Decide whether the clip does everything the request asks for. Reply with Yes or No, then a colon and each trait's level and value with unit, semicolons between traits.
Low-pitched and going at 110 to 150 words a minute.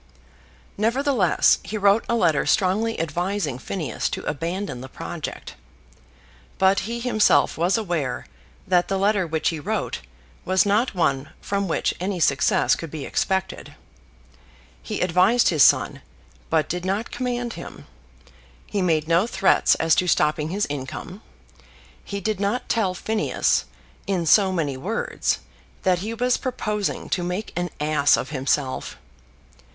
No: medium, 185 Hz; average, 140 wpm